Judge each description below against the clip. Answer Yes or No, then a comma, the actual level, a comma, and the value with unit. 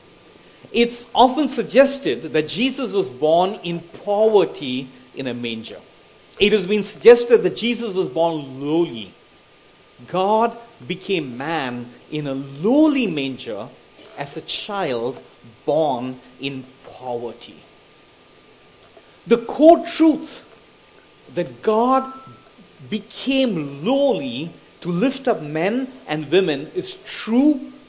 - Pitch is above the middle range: Yes, high, 200 Hz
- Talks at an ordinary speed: No, slow, 105 wpm